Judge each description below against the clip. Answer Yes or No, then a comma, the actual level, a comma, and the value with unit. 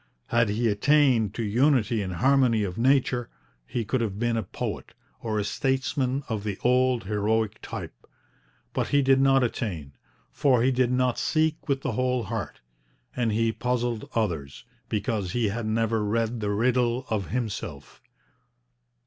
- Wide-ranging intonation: No, average, 3.2 semitones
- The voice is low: Yes, low, 115 Hz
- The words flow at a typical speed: Yes, average, 155 wpm